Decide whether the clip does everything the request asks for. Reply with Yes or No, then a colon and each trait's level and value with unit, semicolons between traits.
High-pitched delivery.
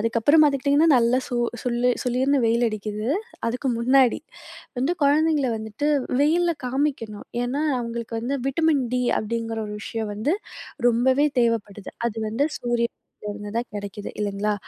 Yes: high, 240 Hz